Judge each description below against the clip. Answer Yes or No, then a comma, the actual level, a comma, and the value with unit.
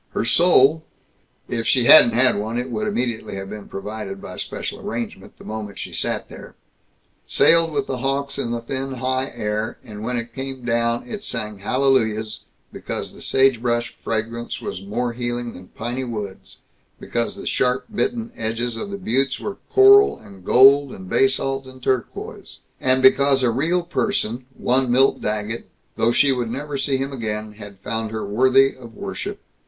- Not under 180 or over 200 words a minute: No, average, 170 wpm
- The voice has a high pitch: No, low, 120 Hz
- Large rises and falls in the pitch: No, average, 3.3 semitones